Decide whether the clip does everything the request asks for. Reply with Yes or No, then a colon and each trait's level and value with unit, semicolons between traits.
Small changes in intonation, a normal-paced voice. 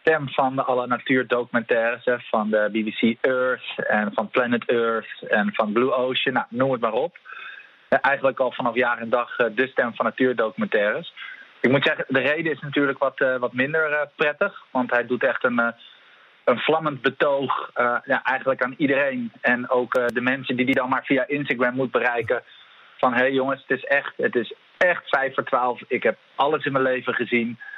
Yes: narrow, 2.3 semitones; average, 190 wpm